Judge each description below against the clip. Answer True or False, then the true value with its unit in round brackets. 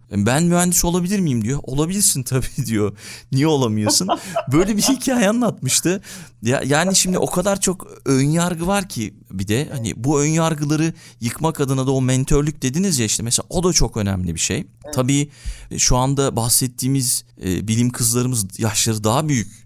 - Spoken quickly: True (160 wpm)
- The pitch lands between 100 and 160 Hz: True (135 Hz)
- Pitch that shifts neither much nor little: False (6.2 semitones)